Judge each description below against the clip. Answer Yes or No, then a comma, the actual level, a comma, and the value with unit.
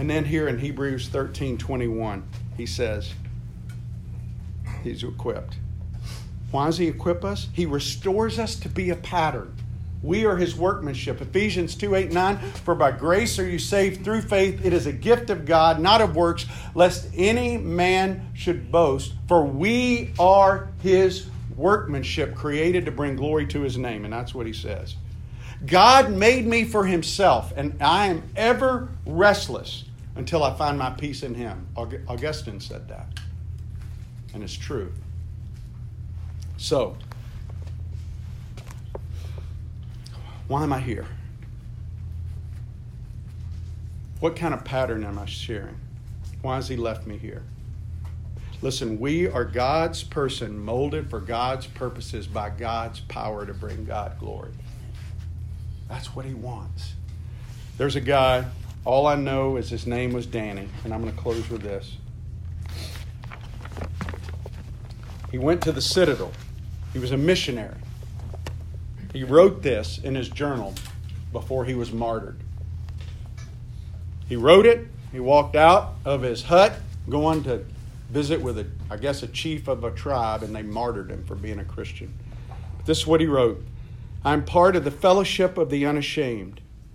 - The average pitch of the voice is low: Yes, low, 115 Hz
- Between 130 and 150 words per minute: Yes, average, 145 wpm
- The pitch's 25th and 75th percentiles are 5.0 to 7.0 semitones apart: Yes, wide, 5.6 semitones